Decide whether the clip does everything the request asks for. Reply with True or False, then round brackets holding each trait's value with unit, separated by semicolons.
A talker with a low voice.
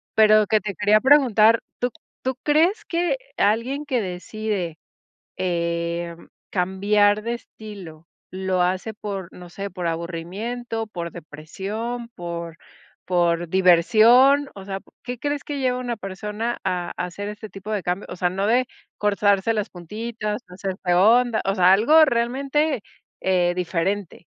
False (205 Hz)